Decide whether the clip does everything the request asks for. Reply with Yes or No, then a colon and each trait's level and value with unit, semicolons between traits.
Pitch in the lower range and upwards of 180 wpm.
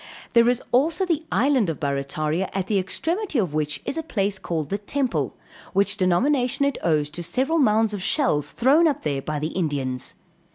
No: high, 200 Hz; average, 190 wpm